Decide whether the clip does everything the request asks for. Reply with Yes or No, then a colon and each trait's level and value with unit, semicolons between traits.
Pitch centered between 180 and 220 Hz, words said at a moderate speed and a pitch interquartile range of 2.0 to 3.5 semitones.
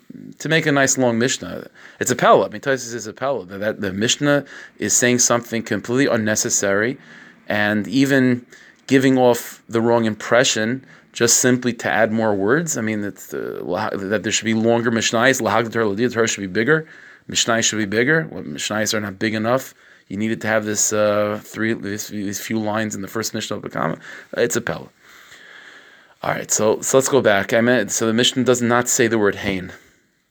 No: low, 115 Hz; average, 190 wpm; average, 2.8 semitones